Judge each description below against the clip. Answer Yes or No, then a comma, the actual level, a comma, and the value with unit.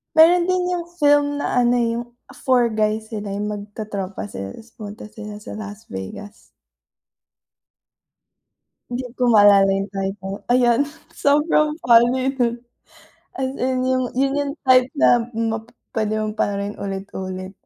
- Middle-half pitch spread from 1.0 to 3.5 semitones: No, average, 4.2 semitones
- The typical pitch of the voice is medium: No, high, 220 Hz